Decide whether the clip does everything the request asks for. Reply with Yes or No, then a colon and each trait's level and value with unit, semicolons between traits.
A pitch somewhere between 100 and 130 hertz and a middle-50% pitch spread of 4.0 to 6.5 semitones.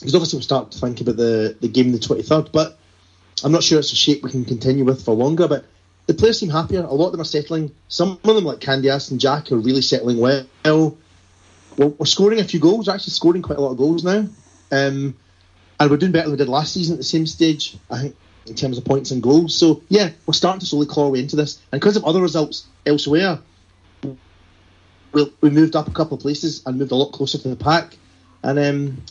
No: medium, 140 Hz; average, 4.3 semitones